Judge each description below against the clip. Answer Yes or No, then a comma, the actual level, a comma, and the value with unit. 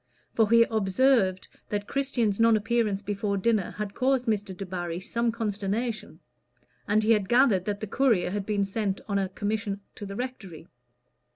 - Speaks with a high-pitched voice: Yes, high, 210 Hz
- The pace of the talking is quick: No, average, 165 wpm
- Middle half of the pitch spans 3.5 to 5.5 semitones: No, average, 2.8 semitones